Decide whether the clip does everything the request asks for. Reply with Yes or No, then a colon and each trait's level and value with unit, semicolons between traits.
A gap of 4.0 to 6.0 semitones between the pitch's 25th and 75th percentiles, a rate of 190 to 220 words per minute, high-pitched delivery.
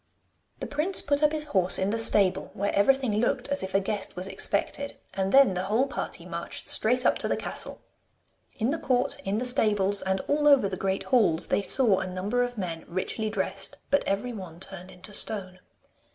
Yes: average, 4.8 semitones; fast, 205 wpm; high, 205 Hz